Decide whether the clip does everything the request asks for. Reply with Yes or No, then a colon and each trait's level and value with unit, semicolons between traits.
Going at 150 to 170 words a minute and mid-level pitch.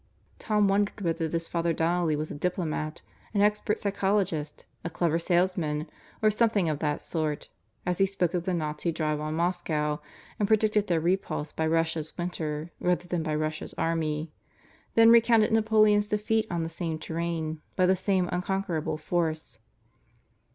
Yes: average, 160 wpm; medium, 170 Hz